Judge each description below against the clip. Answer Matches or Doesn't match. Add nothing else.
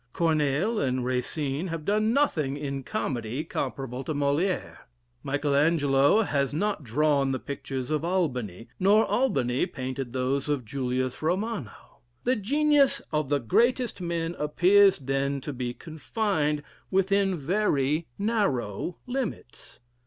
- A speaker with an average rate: Doesn't match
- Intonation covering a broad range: Matches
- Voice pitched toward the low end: Doesn't match